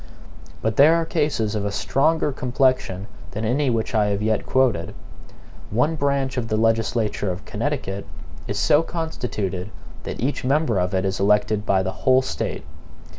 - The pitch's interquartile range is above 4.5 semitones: Yes, average, 5.1 semitones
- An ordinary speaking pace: Yes, average, 165 wpm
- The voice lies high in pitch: No, low, 115 Hz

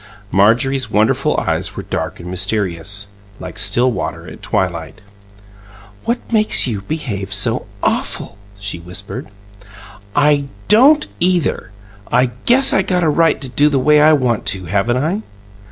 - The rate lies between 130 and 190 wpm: Yes, average, 145 wpm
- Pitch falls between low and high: No, low, 125 Hz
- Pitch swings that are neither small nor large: No, wide, 7.3 semitones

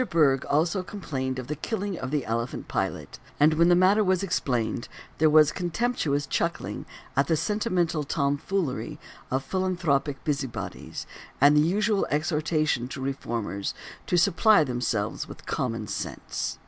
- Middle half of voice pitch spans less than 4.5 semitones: No, average, 5.0 semitones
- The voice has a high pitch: No, medium, 155 Hz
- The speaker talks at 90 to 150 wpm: Yes, average, 140 wpm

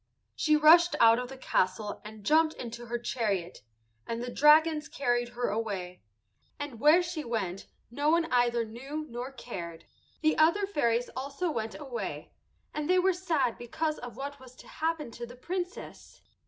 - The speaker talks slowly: No, average, 165 wpm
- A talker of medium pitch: No, very high, 250 Hz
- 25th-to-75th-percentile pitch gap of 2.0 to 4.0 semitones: No, average, 5.1 semitones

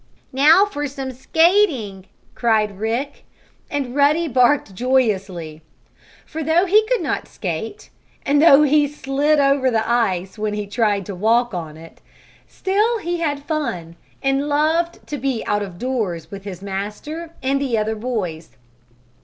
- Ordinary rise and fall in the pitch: No, wide, 6.4 semitones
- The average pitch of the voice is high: Yes, very high, 255 Hz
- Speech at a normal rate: Yes, average, 150 wpm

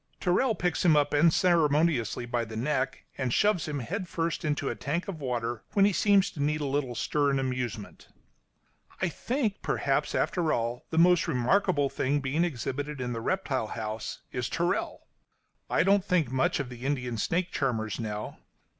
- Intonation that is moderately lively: No, wide, 5.9 semitones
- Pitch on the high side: No, medium, 145 Hz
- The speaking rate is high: No, average, 170 wpm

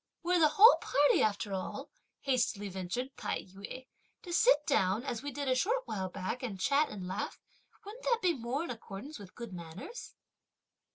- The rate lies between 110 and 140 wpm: No, average, 180 wpm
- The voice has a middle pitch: No, very high, 250 Hz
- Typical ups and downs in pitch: No, wide, 7.6 semitones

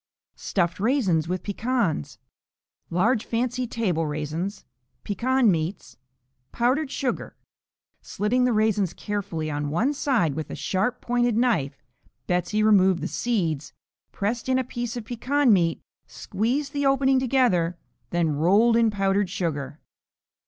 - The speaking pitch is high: Yes, high, 210 Hz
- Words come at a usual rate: No, slow, 130 wpm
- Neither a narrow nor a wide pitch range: No, wide, 6.2 semitones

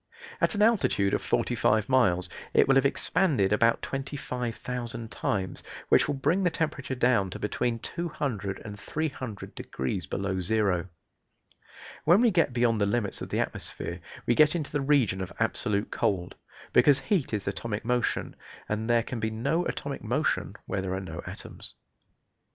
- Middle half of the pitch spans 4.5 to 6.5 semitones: Yes, wide, 5.5 semitones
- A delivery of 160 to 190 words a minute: Yes, average, 165 wpm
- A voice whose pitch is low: Yes, low, 120 Hz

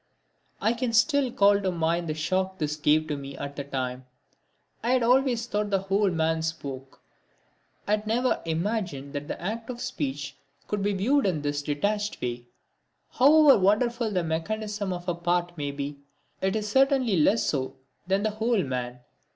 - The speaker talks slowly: No, average, 175 wpm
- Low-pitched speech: No, high, 190 Hz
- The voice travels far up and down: Yes, wide, 6.6 semitones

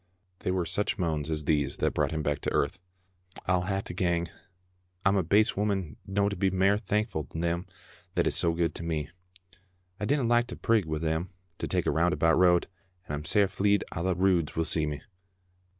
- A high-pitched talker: No, very low, 90 Hz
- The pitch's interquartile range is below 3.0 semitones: No, average, 3.4 semitones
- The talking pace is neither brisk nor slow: No, fast, 215 wpm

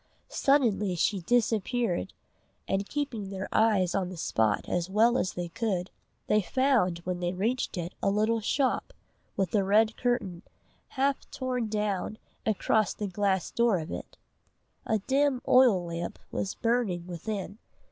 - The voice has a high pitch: Yes, high, 205 Hz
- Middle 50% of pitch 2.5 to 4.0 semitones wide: No, average, 4.5 semitones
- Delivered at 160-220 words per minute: No, average, 145 wpm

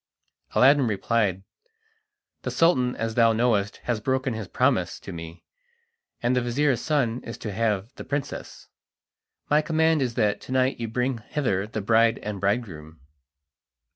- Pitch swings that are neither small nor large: Yes, average, 3.8 semitones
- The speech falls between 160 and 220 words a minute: No, average, 150 wpm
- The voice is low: Yes, low, 115 Hz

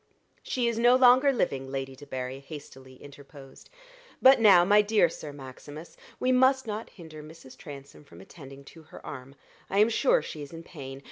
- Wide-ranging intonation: Yes, wide, 8.1 semitones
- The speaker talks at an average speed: Yes, average, 180 wpm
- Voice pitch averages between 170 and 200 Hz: No, medium, 155 Hz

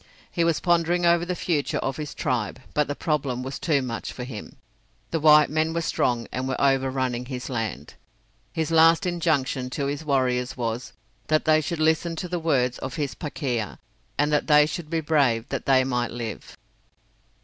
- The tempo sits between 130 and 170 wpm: No, average, 185 wpm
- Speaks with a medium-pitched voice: Yes, medium, 145 Hz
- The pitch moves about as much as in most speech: Yes, average, 4.0 semitones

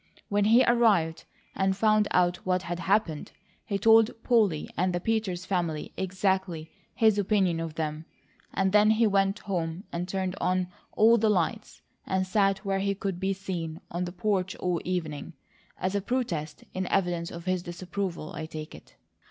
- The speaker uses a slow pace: No, average, 170 wpm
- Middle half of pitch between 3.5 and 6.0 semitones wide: No, average, 2.8 semitones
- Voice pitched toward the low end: No, high, 190 Hz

